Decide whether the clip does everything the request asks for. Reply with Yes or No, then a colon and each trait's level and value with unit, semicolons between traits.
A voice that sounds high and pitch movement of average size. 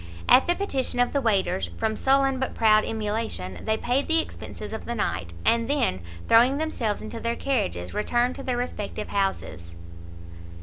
Yes: high, 230 Hz; average, 4.1 semitones